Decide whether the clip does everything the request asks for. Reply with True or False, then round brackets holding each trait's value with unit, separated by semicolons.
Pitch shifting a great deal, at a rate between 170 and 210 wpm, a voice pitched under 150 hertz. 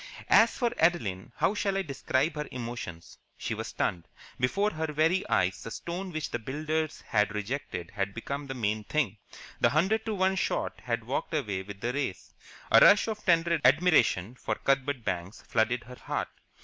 True (7.8 semitones; 180 wpm; 135 Hz)